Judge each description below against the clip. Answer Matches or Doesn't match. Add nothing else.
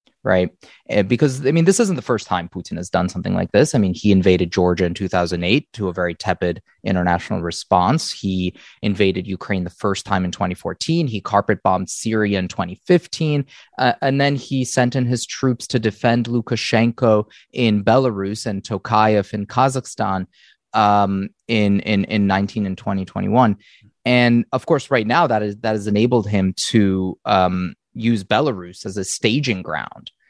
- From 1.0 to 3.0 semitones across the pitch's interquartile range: Doesn't match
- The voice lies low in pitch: Matches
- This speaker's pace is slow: Doesn't match